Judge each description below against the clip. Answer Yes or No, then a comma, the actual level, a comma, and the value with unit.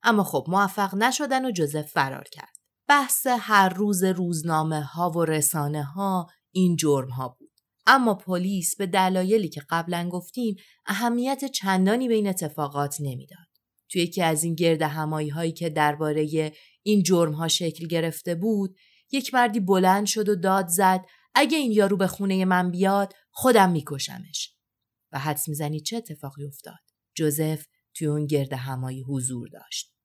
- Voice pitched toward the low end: No, medium, 175 Hz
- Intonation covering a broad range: No, average, 4.6 semitones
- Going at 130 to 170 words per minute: Yes, fast, 155 wpm